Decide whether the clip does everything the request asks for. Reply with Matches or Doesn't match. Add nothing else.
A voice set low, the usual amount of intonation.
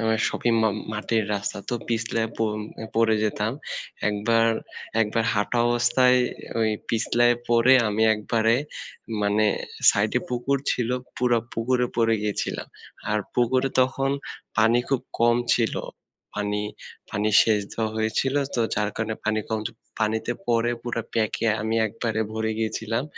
Doesn't match